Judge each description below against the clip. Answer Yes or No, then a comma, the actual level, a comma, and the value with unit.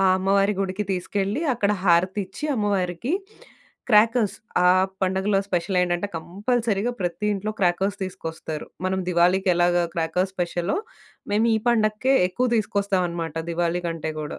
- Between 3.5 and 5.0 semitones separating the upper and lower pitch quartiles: No, average, 2.9 semitones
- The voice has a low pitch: No, high, 190 Hz